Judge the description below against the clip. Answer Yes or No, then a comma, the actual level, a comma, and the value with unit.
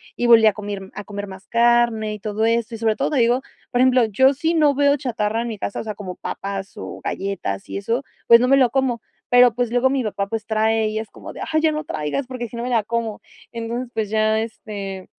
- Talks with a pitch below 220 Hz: No, high, 225 Hz